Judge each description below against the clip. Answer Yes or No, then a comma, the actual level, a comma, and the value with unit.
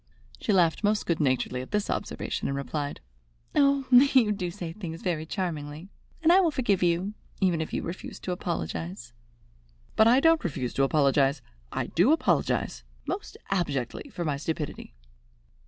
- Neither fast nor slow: Yes, average, 160 wpm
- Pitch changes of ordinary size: No, wide, 6.5 semitones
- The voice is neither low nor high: Yes, medium, 170 Hz